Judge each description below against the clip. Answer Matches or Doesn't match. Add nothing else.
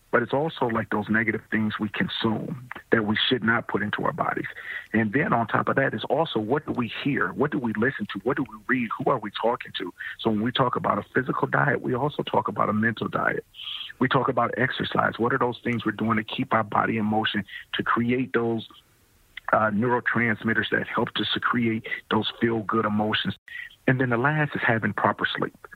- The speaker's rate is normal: Doesn't match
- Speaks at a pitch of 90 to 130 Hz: Matches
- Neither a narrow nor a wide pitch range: Doesn't match